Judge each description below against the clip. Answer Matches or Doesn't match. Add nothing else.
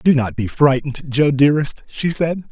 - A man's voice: Matches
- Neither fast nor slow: Matches